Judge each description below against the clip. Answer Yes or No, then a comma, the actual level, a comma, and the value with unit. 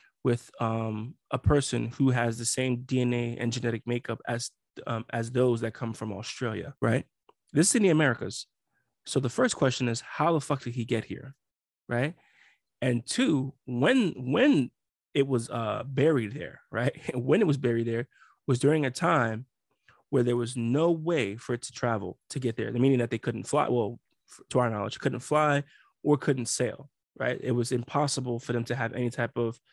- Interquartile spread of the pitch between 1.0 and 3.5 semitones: Yes, average, 3.0 semitones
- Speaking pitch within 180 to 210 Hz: No, low, 125 Hz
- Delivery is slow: No, average, 195 wpm